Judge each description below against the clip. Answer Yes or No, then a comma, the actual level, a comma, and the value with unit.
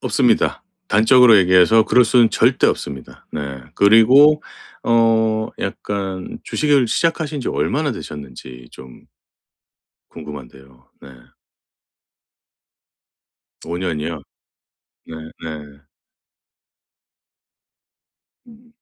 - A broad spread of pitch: Yes, wide, 8.8 semitones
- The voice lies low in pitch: Yes, low, 100 Hz